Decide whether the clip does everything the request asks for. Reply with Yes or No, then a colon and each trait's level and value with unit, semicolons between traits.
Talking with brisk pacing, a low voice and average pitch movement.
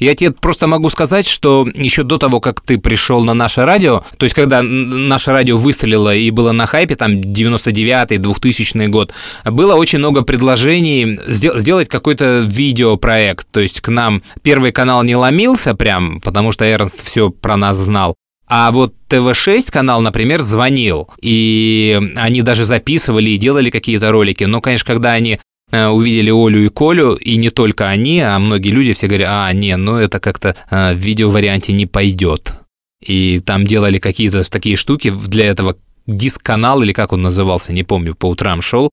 Yes: fast, 170 wpm; low, 110 Hz; average, 3.8 semitones